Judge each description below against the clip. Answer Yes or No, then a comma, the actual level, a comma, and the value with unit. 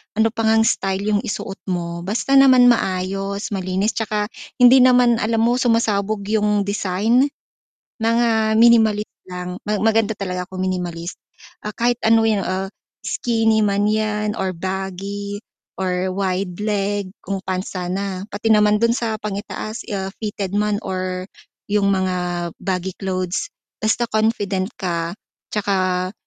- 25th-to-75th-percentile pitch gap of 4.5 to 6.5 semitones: No, average, 2.8 semitones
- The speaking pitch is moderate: No, high, 205 Hz